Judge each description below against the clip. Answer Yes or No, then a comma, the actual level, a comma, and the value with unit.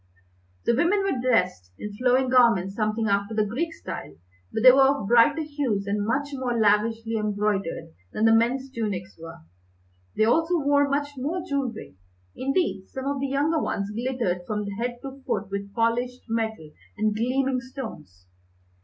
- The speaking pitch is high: Yes, high, 230 Hz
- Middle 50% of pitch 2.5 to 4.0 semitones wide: No, average, 4.5 semitones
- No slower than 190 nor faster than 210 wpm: No, average, 160 wpm